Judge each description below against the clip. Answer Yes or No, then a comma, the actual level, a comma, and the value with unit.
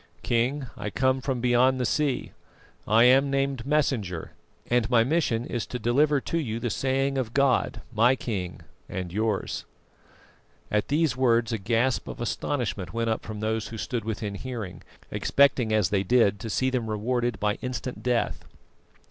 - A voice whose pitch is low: Yes, low, 120 Hz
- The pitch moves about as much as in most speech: Yes, average, 3.2 semitones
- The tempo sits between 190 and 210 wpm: No, average, 165 wpm